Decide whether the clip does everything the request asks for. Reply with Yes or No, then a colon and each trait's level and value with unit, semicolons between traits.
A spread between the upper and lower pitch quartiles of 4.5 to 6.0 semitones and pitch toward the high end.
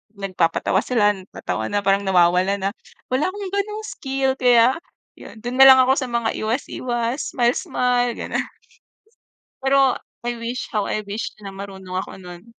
Yes: average, 4.8 semitones; high, 235 Hz